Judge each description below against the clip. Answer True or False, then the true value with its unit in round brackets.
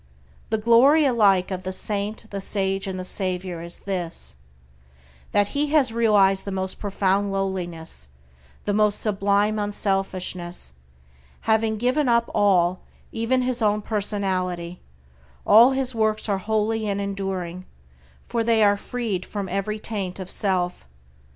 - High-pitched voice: True (200 Hz)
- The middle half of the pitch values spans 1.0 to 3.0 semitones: True (2.7 semitones)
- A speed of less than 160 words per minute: True (140 wpm)